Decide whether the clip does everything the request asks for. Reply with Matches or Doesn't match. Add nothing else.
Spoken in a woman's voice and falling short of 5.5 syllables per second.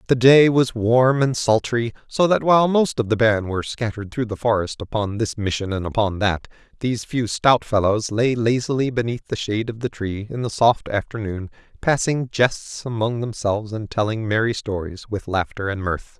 Doesn't match